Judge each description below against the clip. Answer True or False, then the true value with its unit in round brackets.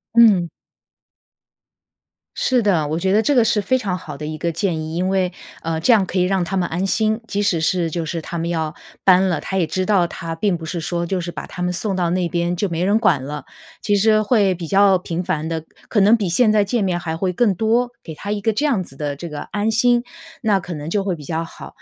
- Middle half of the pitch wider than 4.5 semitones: False (3.7 semitones)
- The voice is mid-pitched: True (180 Hz)